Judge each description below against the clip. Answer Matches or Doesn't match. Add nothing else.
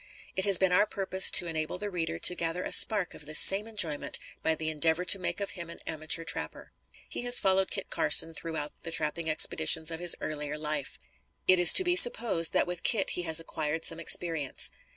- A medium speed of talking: Doesn't match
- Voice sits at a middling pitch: Matches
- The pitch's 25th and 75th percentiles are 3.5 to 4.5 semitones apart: Doesn't match